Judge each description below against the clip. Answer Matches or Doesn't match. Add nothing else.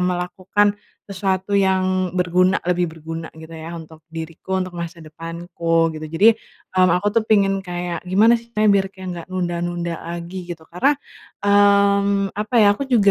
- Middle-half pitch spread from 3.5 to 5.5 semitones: Doesn't match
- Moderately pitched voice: Matches